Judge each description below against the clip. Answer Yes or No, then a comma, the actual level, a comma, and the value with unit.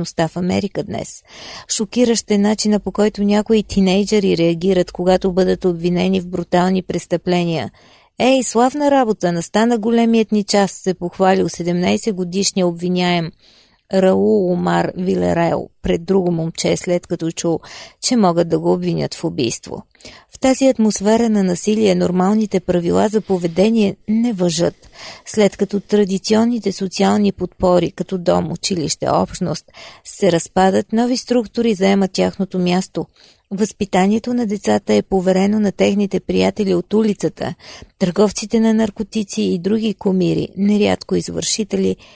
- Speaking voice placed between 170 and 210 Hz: Yes, high, 190 Hz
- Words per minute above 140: No, average, 125 wpm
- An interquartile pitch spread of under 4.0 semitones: Yes, average, 3.1 semitones